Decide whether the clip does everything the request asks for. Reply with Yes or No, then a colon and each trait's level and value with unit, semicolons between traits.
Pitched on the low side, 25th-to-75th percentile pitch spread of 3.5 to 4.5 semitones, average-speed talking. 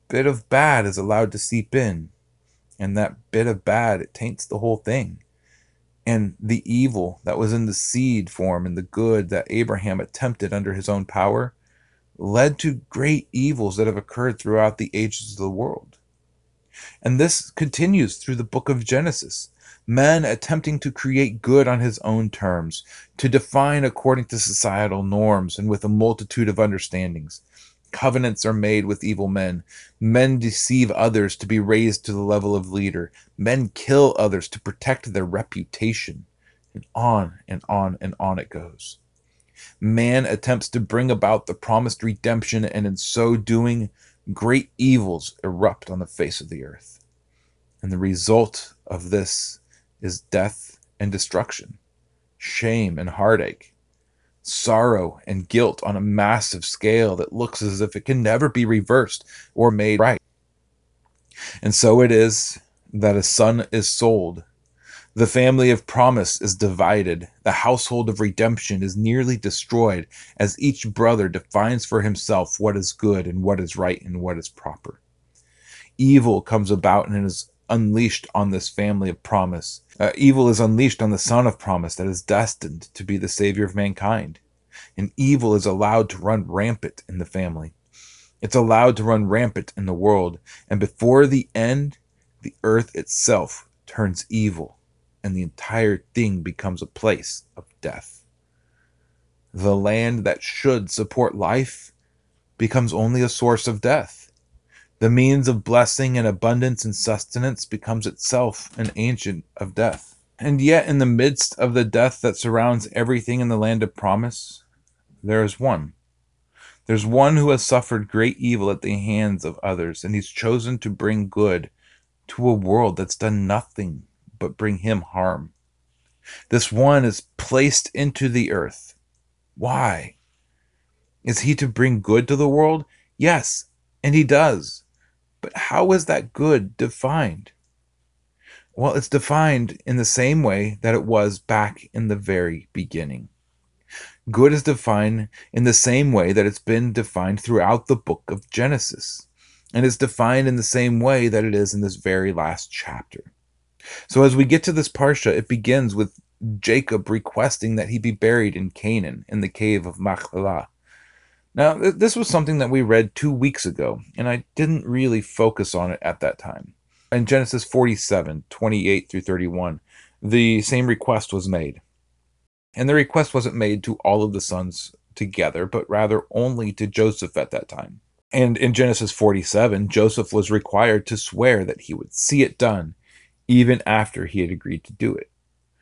Yes: low, 110 Hz; average, 4.2 semitones; average, 165 wpm